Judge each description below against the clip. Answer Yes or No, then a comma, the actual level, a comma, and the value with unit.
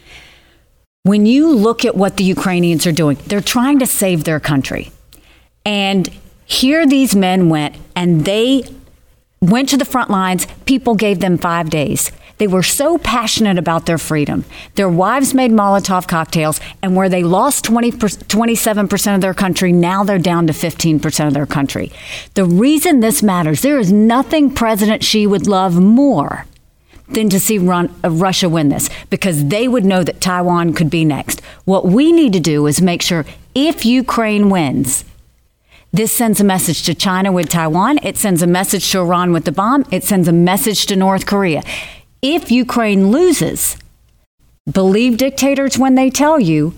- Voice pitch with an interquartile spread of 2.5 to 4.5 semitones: No, average, 5.1 semitones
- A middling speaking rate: Yes, average, 170 wpm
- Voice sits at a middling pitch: No, high, 195 Hz